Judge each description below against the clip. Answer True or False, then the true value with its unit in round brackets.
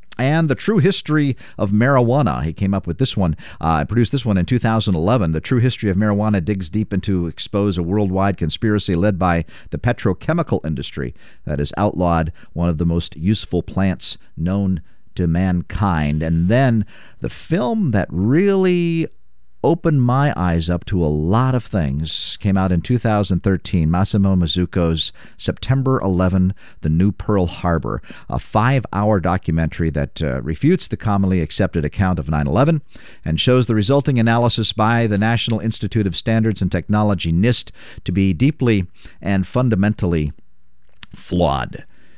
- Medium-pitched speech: False (100 Hz)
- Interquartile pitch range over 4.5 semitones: True (5.0 semitones)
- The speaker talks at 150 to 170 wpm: True (155 wpm)